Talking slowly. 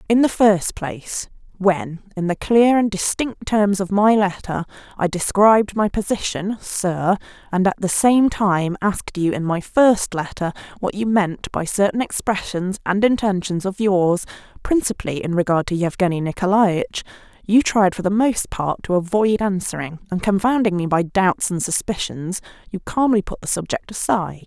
No: average, 165 wpm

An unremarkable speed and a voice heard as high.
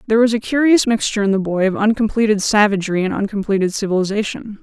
Yes: average, 180 wpm; high, 210 Hz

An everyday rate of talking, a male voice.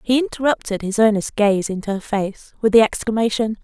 No: average, 180 wpm; female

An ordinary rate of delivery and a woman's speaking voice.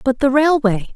Yes: average, 190 wpm; female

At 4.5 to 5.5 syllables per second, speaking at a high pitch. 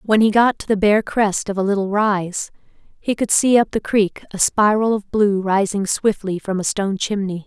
Yes: 4.8 syllables/s; high, 205 Hz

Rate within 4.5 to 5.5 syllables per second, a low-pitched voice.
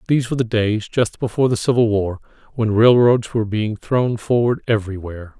No: 5.9 syllables/s; low, 115 Hz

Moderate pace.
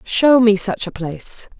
Yes: average, 190 wpm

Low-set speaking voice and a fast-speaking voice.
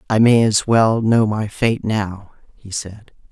No: low, 110 Hz; average, 180 wpm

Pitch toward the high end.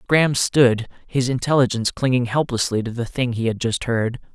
No: low, 125 Hz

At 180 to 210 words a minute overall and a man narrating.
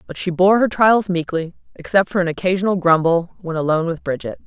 No: average, 200 wpm; female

